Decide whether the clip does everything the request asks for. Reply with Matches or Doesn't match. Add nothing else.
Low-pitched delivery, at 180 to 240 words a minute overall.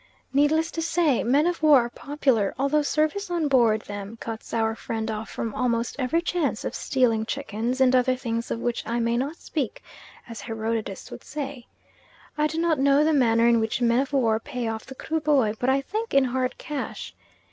Doesn't match